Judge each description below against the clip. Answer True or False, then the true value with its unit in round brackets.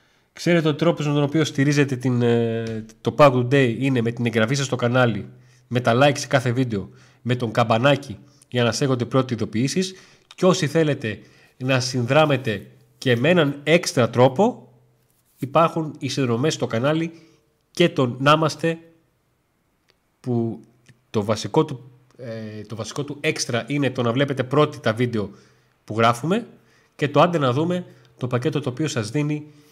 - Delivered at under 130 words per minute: False (160 wpm)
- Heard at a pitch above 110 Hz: True (135 Hz)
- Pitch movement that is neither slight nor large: True (4.2 semitones)